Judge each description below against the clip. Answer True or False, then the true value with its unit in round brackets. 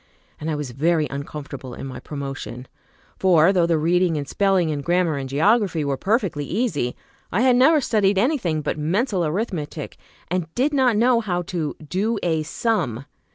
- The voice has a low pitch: False (170 Hz)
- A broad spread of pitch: True (5.9 semitones)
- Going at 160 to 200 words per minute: True (175 wpm)